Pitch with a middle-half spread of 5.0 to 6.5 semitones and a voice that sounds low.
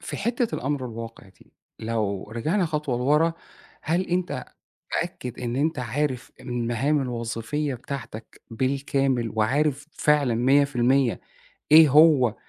No: average, 4.1 semitones; low, 130 Hz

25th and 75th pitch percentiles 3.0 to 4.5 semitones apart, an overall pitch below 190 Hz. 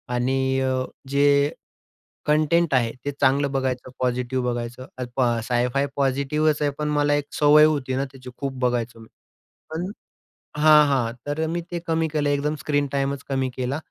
No: narrow, 2.6 semitones; medium, 140 Hz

